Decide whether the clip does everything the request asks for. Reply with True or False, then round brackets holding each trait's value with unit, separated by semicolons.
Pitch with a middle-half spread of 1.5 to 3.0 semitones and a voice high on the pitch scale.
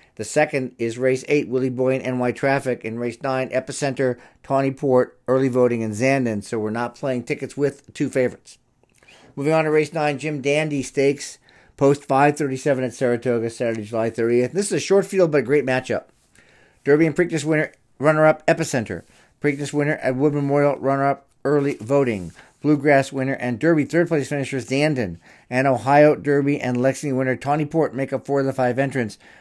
False (2.7 semitones; 135 Hz)